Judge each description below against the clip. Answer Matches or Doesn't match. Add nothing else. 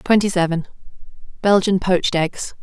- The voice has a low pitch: Doesn't match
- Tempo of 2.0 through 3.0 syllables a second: Doesn't match